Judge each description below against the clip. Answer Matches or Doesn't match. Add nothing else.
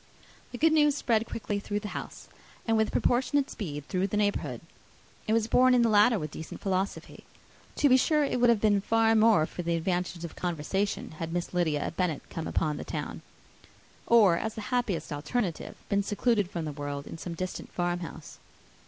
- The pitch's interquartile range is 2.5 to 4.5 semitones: Doesn't match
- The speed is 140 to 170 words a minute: Doesn't match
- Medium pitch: Doesn't match